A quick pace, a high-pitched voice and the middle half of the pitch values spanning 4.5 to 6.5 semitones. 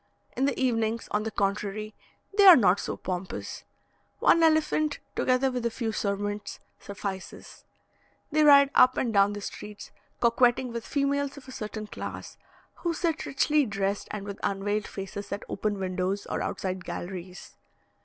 No: average, 155 wpm; high, 215 Hz; average, 5.1 semitones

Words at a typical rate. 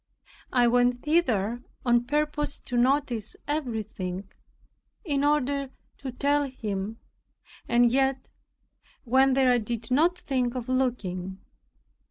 No: slow, 110 wpm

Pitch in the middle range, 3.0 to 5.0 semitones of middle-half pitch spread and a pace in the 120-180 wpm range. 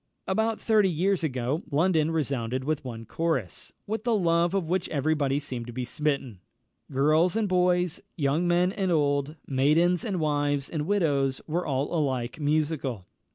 Yes: medium, 155 Hz; average, 4.4 semitones; average, 160 wpm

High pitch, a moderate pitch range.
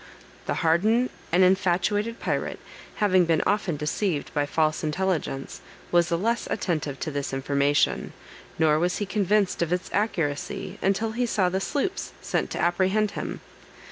No: medium, 180 Hz; average, 4.9 semitones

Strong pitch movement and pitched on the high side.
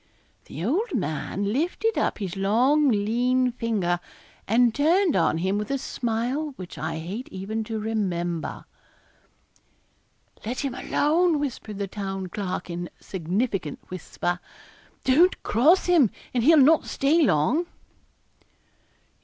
Yes: wide, 6.9 semitones; high, 225 Hz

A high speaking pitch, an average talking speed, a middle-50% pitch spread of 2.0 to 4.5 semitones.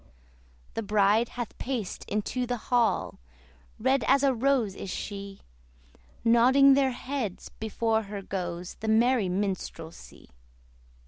No: high, 225 Hz; slow, 120 wpm; average, 4.1 semitones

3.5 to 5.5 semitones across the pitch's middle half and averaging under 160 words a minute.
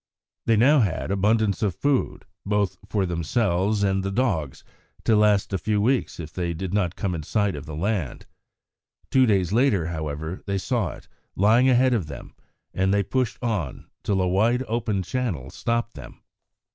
No: average, 4.4 semitones; average, 175 wpm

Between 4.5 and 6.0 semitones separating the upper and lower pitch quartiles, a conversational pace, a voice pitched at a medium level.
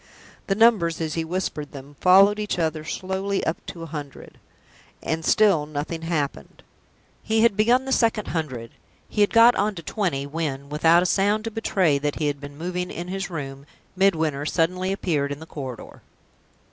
Yes: average, 4.9 semitones; average, 180 wpm; medium, 165 Hz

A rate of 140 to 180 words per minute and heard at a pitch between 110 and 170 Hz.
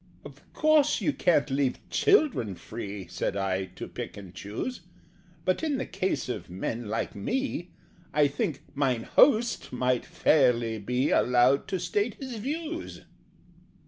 Yes: average, 145 wpm; medium, 140 Hz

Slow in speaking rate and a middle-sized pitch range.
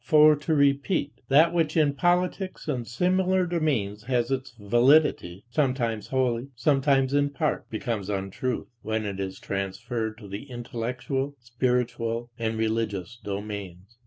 Yes: slow, 130 wpm; average, 4.5 semitones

